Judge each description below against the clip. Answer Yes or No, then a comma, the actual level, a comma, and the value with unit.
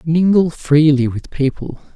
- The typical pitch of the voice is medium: Yes, medium, 150 Hz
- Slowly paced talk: Yes, slow, 125 wpm